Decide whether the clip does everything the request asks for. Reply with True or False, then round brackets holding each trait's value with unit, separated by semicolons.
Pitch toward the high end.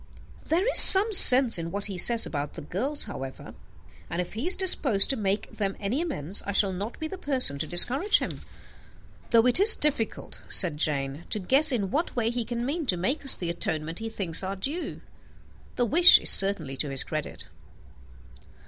True (215 Hz)